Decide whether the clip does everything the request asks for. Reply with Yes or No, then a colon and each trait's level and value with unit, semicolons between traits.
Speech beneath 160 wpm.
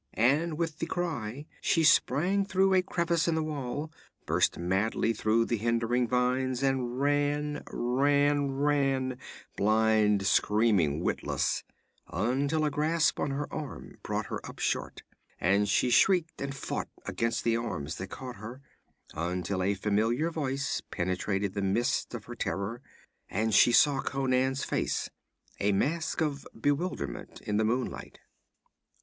Yes: average, 145 wpm